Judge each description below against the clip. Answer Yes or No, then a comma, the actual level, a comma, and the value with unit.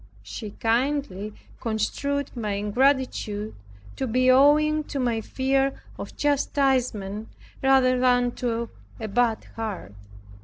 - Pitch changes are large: No, average, 3.7 semitones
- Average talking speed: No, slow, 110 wpm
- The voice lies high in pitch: Yes, high, 245 Hz